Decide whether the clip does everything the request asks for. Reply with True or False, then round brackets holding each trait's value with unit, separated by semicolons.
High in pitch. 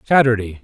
False (115 Hz)